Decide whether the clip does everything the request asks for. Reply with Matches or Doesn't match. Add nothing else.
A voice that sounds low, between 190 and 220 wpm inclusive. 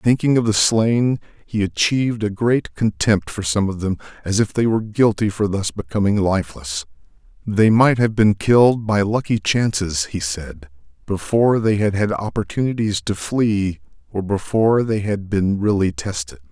Doesn't match